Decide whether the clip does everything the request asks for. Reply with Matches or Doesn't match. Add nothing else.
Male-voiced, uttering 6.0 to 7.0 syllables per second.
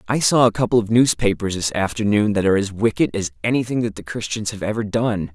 Matches